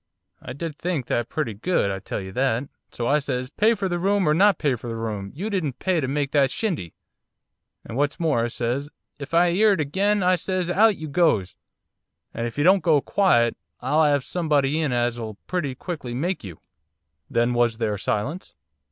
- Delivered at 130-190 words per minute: No, fast, 205 wpm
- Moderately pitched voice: Yes, medium, 145 Hz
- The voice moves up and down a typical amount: No, wide, 6.8 semitones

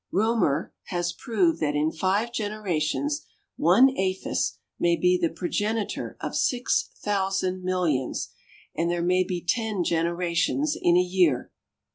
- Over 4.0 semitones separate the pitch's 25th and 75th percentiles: No, average, 3.6 semitones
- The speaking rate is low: Yes, slow, 130 wpm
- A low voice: No, medium, 180 Hz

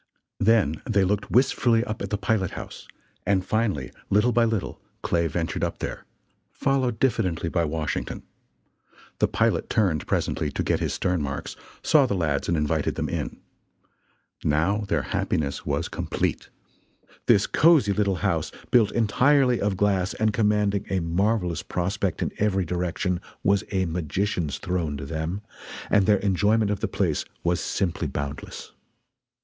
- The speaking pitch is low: Yes, very low, 95 Hz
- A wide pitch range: No, average, 4.1 semitones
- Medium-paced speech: Yes, average, 150 wpm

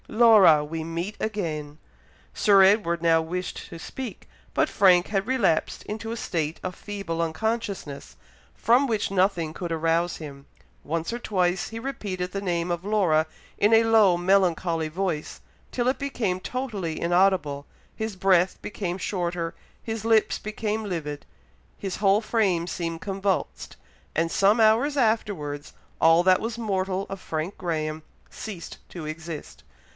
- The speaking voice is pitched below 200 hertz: Yes, medium, 185 Hz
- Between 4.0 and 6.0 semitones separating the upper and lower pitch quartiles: Yes, average, 4.3 semitones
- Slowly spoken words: No, average, 145 wpm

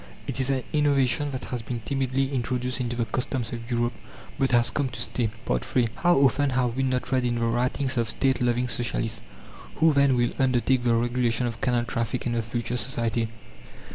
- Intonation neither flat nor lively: No, narrow, 1.9 semitones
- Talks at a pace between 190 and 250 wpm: Yes, average, 200 wpm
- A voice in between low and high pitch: No, low, 125 Hz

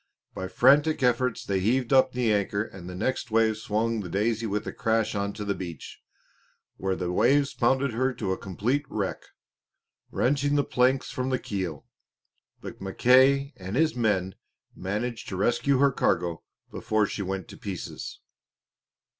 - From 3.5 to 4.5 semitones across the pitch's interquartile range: No, average, 5.1 semitones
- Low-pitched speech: Yes, low, 110 Hz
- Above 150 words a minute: Yes, average, 160 wpm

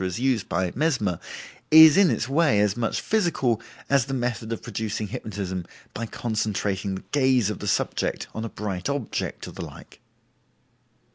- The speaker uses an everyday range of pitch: Yes, average, 4.8 semitones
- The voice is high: No, low, 115 Hz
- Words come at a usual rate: Yes, average, 165 wpm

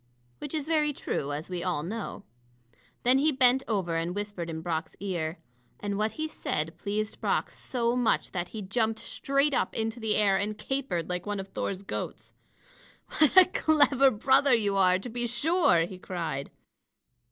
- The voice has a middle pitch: No, high, 210 Hz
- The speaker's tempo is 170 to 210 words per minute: Yes, average, 175 wpm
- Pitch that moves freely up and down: Yes, wide, 6.5 semitones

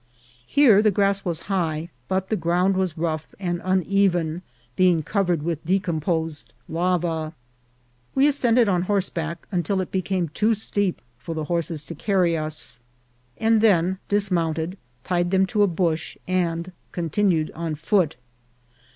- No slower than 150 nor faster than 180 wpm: No, average, 140 wpm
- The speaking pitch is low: No, medium, 180 Hz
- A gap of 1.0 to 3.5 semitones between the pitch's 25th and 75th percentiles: Yes, average, 3.1 semitones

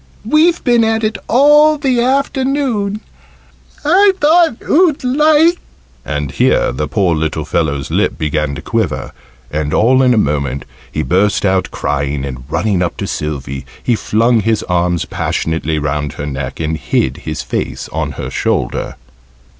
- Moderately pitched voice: No, very low, 95 Hz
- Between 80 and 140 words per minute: No, average, 155 wpm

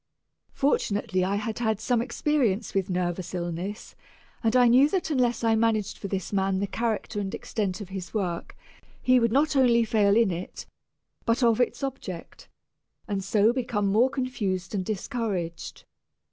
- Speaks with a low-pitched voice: No, high, 215 Hz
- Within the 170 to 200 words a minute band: No, average, 160 wpm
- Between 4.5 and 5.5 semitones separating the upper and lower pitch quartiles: No, average, 3.8 semitones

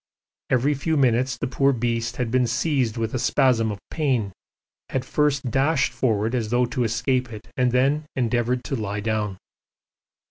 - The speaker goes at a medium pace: Yes, average, 170 wpm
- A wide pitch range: No, average, 2.8 semitones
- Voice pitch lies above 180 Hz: No, low, 125 Hz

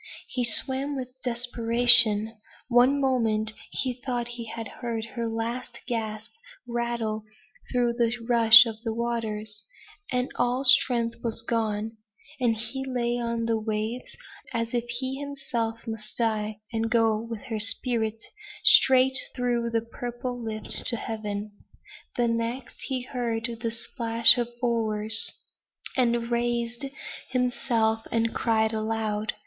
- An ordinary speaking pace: No, slow, 130 wpm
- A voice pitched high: Yes, high, 235 Hz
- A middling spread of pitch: No, narrow, 1.7 semitones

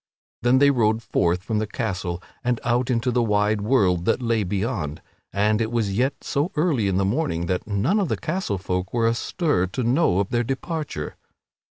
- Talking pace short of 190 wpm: No, average, 195 wpm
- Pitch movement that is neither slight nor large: Yes, average, 4.7 semitones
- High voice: No, low, 115 Hz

